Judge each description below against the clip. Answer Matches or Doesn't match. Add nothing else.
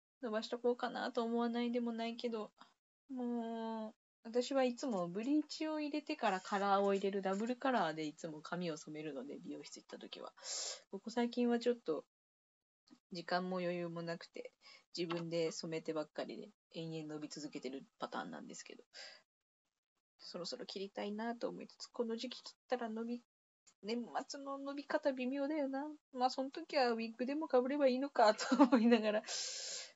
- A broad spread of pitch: Matches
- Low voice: Doesn't match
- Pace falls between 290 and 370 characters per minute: Matches